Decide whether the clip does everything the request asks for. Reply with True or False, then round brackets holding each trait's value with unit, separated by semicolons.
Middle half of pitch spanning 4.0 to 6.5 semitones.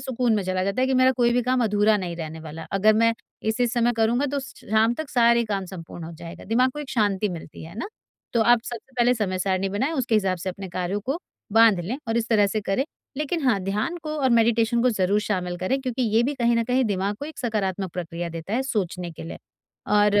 True (4.4 semitones)